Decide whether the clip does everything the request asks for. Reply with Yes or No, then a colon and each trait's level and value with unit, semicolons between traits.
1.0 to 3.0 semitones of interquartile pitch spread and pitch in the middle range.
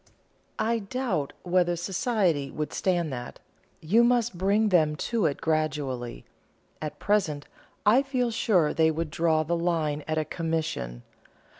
No: wide, 5.4 semitones; medium, 165 Hz